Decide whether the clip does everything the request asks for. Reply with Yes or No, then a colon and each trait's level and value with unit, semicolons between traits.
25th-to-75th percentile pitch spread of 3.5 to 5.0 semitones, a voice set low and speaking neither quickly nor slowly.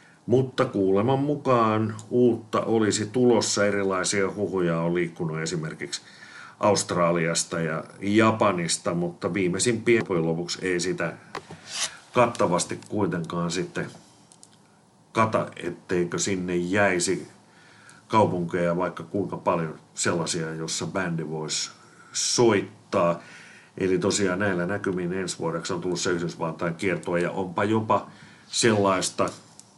Yes: average, 3.9 semitones; very low, 95 Hz; average, 105 wpm